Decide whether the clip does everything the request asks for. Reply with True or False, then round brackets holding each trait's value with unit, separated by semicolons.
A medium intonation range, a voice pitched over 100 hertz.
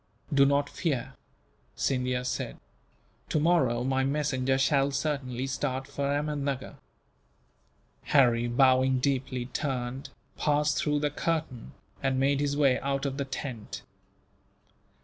False (1.9 semitones; 135 Hz)